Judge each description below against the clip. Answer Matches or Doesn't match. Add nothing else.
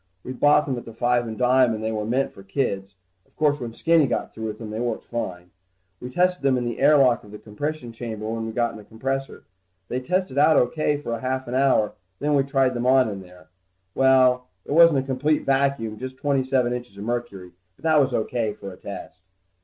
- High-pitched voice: Doesn't match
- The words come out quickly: Matches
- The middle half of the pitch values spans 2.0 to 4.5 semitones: Matches